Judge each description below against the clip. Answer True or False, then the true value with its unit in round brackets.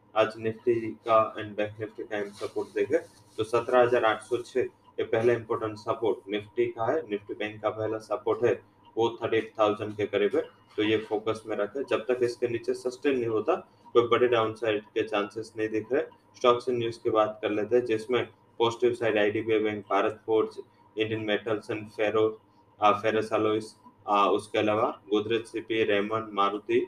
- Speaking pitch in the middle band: False (110 Hz)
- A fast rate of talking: False (185 wpm)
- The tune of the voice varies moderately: False (2.0 semitones)